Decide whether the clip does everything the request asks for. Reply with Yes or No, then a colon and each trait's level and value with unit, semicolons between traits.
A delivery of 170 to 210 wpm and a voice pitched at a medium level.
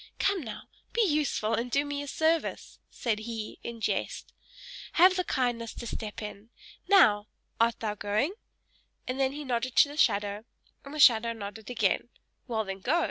No: average, 175 wpm; high, 235 Hz